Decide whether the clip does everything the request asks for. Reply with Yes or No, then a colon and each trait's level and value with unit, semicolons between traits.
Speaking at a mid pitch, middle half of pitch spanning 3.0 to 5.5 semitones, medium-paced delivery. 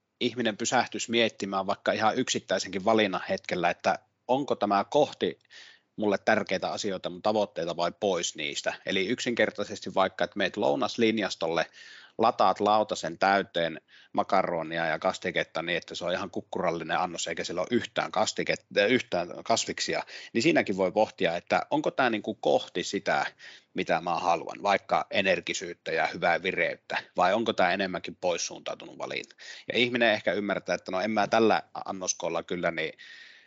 No: low, 110 Hz; average, 3.5 semitones; average, 145 wpm